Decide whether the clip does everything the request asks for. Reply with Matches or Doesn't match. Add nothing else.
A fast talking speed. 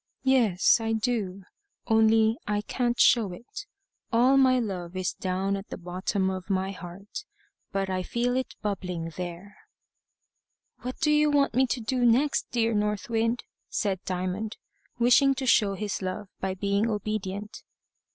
Doesn't match